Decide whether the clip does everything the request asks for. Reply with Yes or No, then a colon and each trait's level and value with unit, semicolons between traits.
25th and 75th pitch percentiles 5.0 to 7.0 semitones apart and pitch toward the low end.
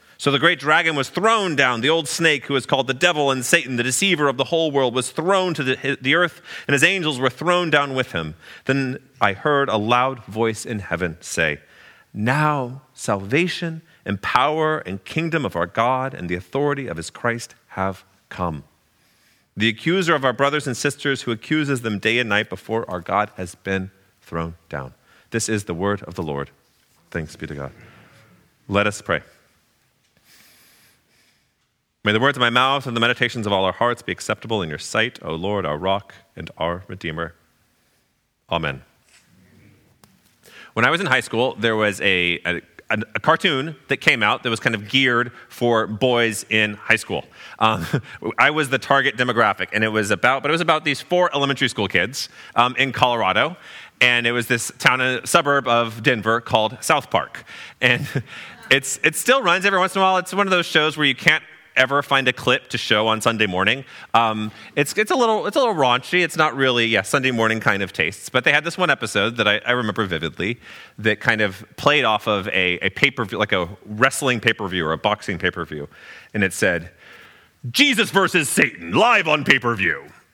Yes: wide, 5.6 semitones; low, 125 Hz